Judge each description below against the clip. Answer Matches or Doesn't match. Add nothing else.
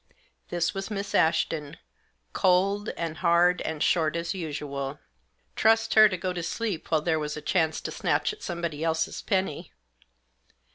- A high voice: Doesn't match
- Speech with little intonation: Doesn't match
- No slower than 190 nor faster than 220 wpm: Doesn't match